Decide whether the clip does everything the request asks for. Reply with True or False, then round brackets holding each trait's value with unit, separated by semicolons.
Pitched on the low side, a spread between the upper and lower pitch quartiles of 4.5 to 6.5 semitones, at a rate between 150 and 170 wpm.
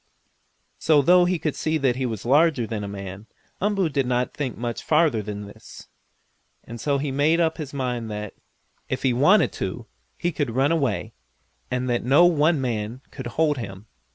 False (130 Hz; 5.2 semitones; 190 wpm)